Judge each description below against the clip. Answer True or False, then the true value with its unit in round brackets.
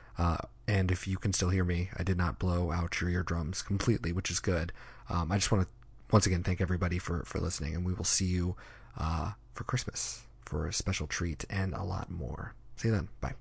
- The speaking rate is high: True (230 wpm)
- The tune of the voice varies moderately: True (3.5 semitones)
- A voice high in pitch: False (95 Hz)